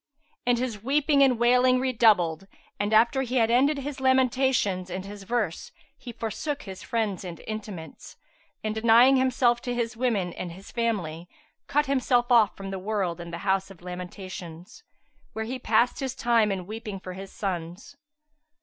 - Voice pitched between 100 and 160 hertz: No, high, 220 Hz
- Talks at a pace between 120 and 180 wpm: Yes, average, 170 wpm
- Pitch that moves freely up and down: No, average, 4.9 semitones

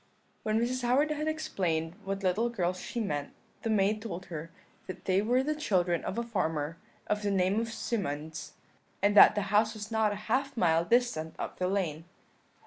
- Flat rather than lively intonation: No, average, 4.9 semitones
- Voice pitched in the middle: No, high, 205 Hz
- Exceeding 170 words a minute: Yes, average, 190 wpm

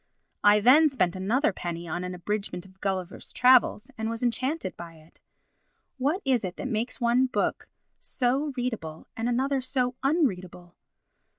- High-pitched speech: Yes, high, 230 Hz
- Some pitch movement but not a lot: No, wide, 6.1 semitones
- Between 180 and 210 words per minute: No, average, 155 wpm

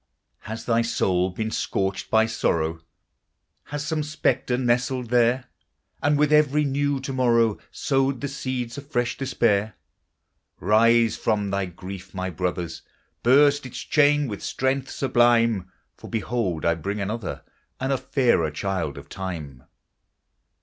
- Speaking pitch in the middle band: No, low, 115 Hz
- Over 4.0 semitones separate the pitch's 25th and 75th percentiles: Yes, wide, 5.6 semitones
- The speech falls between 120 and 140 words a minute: Yes, slow, 135 wpm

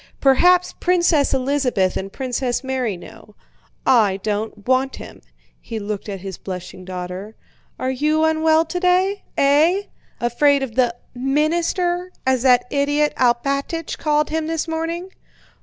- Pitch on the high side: Yes, very high, 270 Hz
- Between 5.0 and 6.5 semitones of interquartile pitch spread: Yes, wide, 5.5 semitones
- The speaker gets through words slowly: Yes, slow, 130 wpm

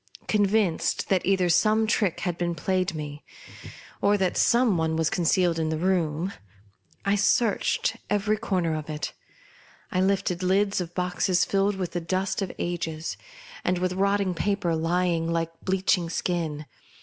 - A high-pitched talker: No, medium, 180 Hz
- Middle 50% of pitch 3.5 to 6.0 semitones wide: No, average, 2.9 semitones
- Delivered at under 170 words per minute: Yes, average, 155 wpm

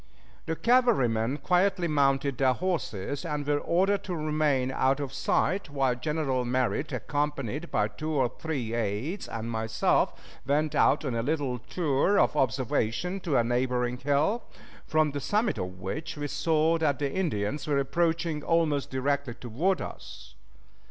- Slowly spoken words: No, average, 150 wpm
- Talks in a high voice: No, medium, 145 Hz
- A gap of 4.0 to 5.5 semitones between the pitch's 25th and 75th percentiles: Yes, average, 4.3 semitones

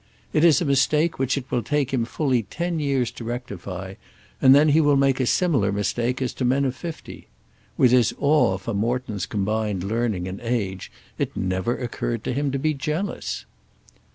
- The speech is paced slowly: No, average, 185 wpm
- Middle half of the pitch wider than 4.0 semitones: Yes, average, 4.7 semitones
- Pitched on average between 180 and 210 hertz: No, low, 125 Hz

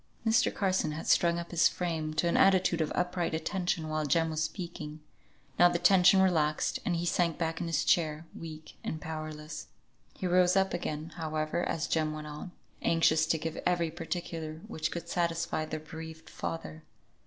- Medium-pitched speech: Yes, medium, 165 Hz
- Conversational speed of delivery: Yes, average, 175 wpm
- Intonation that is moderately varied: No, narrow, 2.1 semitones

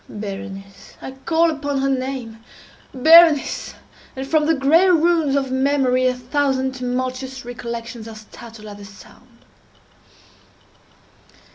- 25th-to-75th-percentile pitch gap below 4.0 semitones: Yes, average, 3.3 semitones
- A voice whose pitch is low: No, very high, 260 Hz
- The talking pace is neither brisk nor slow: No, slow, 105 wpm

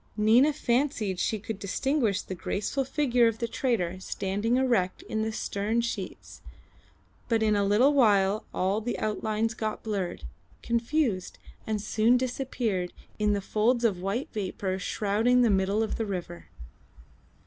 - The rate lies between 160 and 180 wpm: No, average, 150 wpm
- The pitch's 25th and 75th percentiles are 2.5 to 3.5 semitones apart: Yes, average, 3.2 semitones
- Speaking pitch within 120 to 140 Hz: No, high, 215 Hz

